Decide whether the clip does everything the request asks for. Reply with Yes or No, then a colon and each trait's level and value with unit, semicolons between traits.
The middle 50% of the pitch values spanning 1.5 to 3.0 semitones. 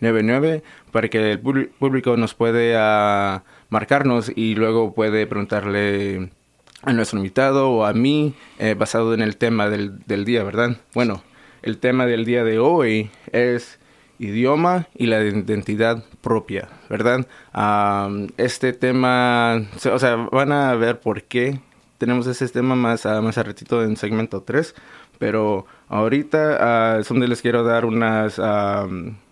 Yes: average, 2.7 semitones